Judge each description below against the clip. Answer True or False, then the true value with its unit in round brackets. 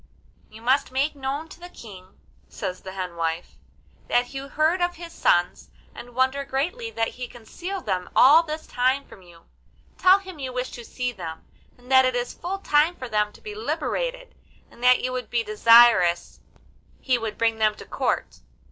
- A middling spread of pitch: False (6.1 semitones)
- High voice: True (255 Hz)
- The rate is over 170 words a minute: True (190 wpm)